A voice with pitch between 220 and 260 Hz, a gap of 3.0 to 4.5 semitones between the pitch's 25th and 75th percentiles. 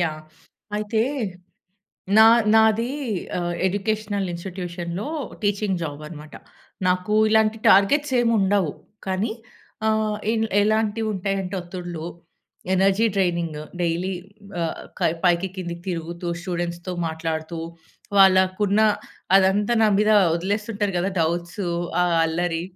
No: high, 190 Hz; average, 3.4 semitones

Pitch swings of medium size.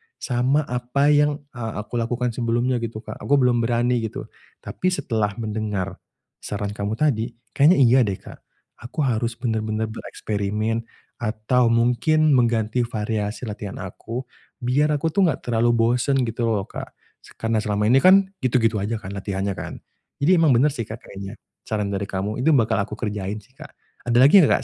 Yes: average, 3.1 semitones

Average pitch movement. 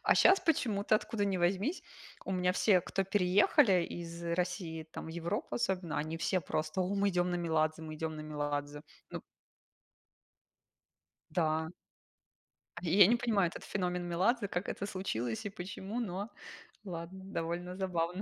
Yes: average, 3.1 semitones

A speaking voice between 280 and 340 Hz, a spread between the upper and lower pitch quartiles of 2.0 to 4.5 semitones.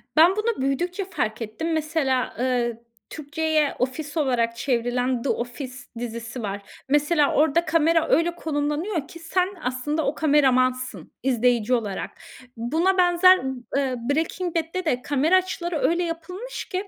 No: very high, 295 Hz; average, 4.9 semitones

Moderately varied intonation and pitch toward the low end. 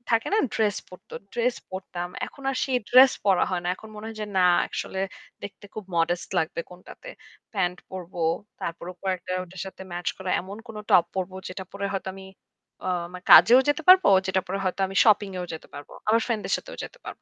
No: average, 3.4 semitones; high, 190 Hz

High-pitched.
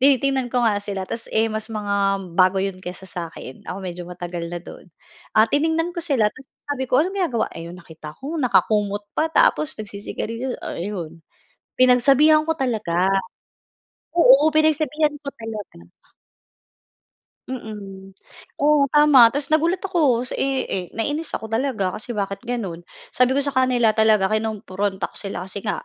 Yes: high, 225 Hz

